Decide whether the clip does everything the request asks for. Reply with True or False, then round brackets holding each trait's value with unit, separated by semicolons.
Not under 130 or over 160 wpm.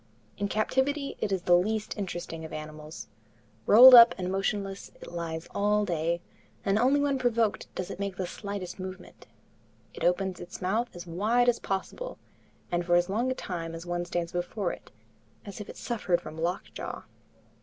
False (175 wpm)